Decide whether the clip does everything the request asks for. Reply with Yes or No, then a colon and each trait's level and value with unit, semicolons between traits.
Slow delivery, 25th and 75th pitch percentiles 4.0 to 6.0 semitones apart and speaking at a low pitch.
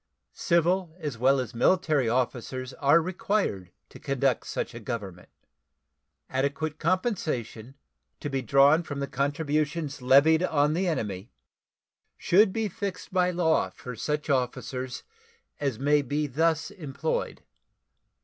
No: slow, 120 wpm; average, 4.4 semitones; medium, 145 Hz